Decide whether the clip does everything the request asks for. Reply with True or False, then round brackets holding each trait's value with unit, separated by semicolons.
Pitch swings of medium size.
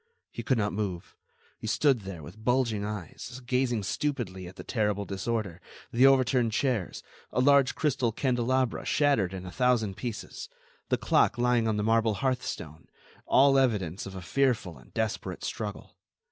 True (4.7 semitones)